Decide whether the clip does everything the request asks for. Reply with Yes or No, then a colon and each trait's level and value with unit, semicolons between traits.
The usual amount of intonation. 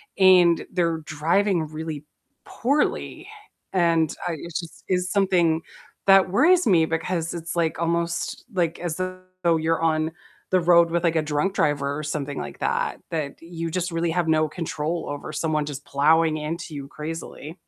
No: narrow, 2.1 semitones